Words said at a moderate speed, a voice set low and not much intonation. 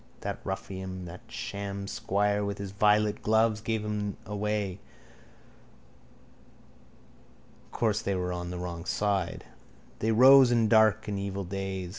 No: slow, 130 wpm; low, 100 Hz; narrow, 2.0 semitones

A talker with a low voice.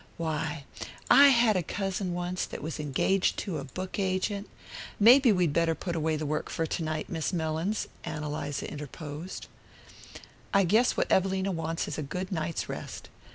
No: medium, 170 Hz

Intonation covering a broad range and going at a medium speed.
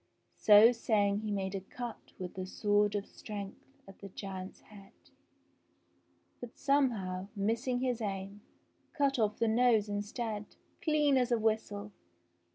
No: average, 3.1 semitones; average, 150 wpm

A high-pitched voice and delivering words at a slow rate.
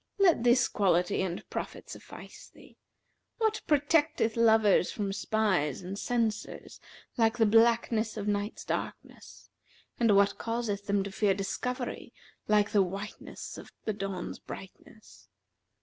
Yes: high, 210 Hz; slow, 130 wpm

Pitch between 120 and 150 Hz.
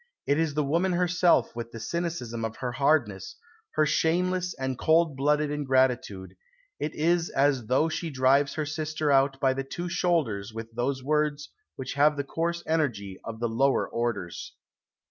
Yes: medium, 140 Hz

